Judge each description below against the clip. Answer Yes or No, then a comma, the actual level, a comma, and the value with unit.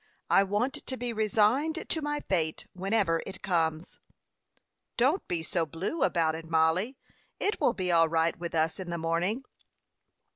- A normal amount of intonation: No, wide, 6.2 semitones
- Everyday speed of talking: Yes, average, 160 wpm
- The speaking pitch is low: No, medium, 185 Hz